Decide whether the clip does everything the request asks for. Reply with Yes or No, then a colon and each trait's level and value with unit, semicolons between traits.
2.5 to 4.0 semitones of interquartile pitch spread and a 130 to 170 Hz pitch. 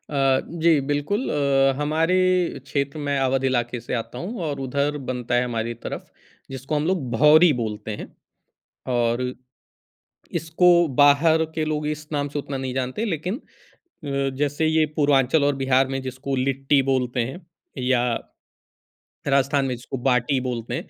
Yes: average, 2.8 semitones; medium, 140 Hz